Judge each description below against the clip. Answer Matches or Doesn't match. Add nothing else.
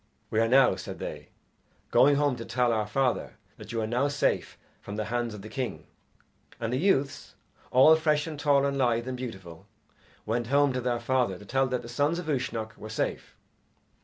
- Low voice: Matches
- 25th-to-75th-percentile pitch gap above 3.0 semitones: Matches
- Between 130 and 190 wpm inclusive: Doesn't match